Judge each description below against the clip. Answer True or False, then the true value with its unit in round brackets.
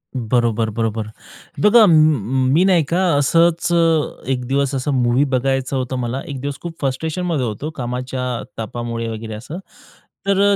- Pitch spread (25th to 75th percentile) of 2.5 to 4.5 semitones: False (5.0 semitones)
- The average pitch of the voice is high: False (130 Hz)